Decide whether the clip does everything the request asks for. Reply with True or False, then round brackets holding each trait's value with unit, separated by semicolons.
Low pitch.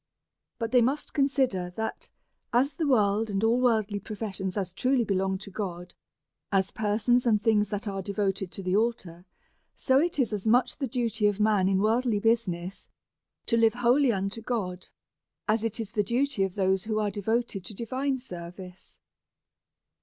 False (215 Hz)